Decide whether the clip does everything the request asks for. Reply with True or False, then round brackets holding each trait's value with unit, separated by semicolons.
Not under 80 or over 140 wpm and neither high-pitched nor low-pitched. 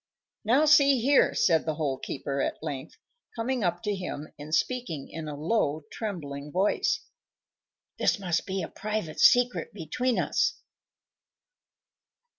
True (135 wpm; 175 Hz)